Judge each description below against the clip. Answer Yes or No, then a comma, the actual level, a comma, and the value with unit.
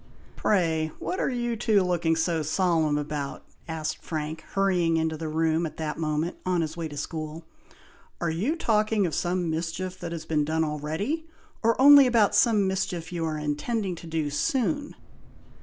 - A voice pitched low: No, medium, 165 Hz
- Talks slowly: No, average, 175 wpm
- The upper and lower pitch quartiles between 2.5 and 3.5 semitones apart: No, average, 3.9 semitones